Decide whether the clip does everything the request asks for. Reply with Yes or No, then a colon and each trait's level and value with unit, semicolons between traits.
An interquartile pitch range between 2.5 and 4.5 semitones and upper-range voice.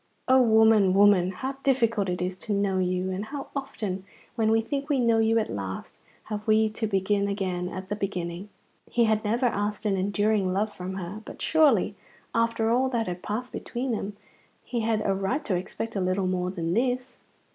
Yes: average, 3.4 semitones; high, 210 Hz